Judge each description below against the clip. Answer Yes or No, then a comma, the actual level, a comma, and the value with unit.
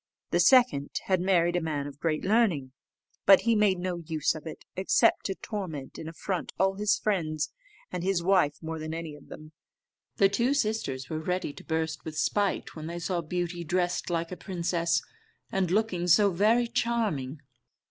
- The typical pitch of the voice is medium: Yes, medium, 175 Hz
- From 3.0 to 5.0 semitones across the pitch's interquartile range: Yes, average, 3.6 semitones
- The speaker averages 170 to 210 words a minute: Yes, average, 180 wpm